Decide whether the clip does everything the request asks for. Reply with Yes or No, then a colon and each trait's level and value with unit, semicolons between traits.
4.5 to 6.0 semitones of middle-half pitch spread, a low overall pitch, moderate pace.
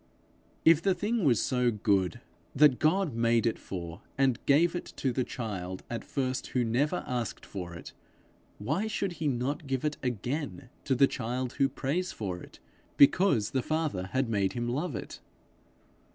Yes: average, 4.8 semitones; low, 130 Hz; average, 170 wpm